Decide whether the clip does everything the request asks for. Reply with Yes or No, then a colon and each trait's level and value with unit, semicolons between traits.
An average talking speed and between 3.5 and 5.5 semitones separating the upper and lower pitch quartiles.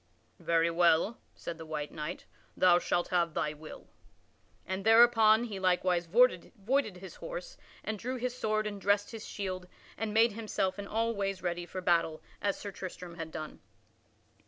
Yes: average, 165 wpm; average, 4.3 semitones